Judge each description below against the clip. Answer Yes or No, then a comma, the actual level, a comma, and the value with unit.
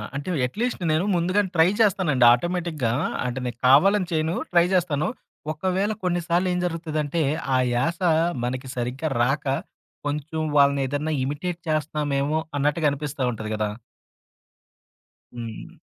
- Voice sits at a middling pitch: Yes, medium, 155 Hz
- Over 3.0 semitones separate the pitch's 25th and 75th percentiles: Yes, average, 4.1 semitones